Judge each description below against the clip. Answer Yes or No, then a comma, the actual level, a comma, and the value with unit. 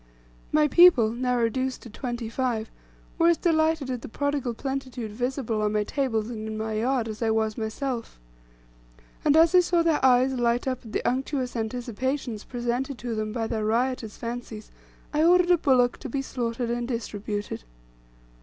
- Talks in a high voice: Yes, high, 245 Hz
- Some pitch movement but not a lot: Yes, average, 3.3 semitones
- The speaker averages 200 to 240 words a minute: No, average, 175 wpm